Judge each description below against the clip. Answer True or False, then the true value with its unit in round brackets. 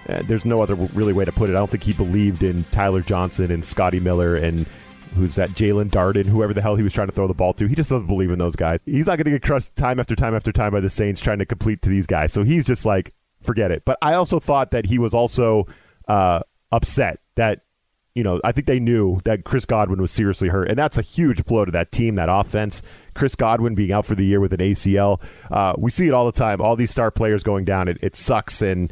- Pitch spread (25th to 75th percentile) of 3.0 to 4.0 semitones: True (3.7 semitones)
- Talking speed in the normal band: False (265 wpm)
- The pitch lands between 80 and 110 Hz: True (105 Hz)